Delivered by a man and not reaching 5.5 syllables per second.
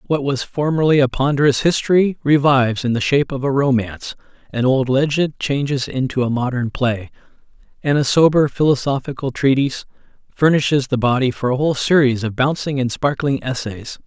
No: male; 5.6 syllables/s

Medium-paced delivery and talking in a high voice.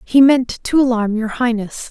Yes: average, 190 wpm; high, 240 Hz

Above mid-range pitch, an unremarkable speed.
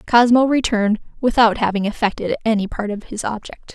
Yes: high, 220 Hz; average, 160 wpm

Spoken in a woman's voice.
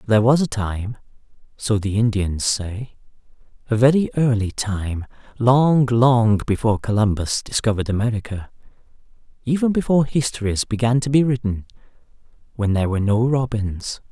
No: male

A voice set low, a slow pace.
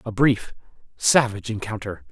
Yes: low, 110 Hz; slow, 115 wpm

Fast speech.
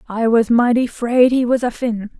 Yes: fast, 220 wpm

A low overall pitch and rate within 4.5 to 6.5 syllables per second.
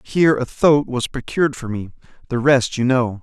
Yes: low, 130 Hz; 5.1 syllables/s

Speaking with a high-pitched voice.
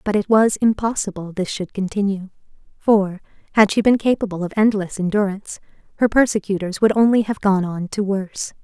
Yes: high, 200 Hz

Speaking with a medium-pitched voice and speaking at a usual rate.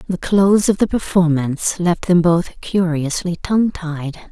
Yes: medium, 175 Hz; average, 155 wpm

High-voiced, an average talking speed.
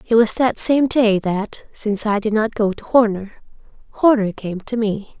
Yes: high, 220 Hz; average, 195 wpm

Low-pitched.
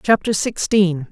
No: high, 190 Hz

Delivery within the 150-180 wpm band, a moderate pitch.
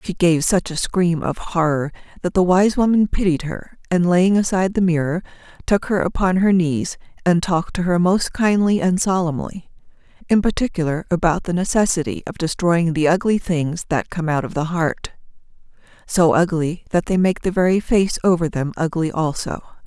Yes: average, 175 wpm; medium, 175 Hz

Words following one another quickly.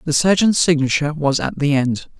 No: average, 190 wpm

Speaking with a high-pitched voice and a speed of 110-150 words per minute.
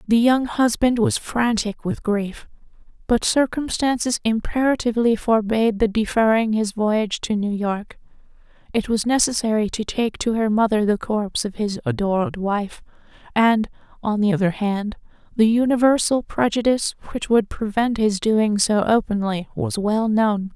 Yes: high, 220 Hz; average, 145 wpm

